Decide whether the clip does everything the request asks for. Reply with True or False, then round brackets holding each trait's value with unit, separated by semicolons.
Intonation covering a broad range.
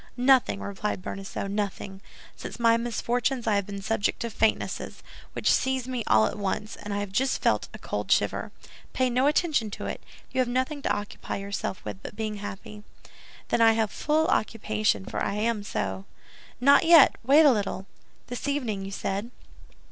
False (4.1 semitones)